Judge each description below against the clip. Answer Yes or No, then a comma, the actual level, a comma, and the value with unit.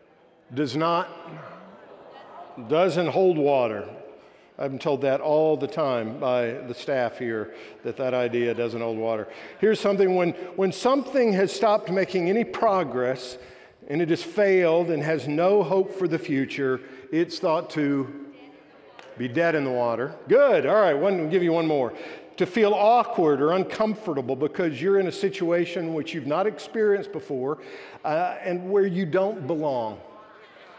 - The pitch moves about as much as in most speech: No, wide, 6.0 semitones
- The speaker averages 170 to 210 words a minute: No, average, 155 wpm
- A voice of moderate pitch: Yes, medium, 165 Hz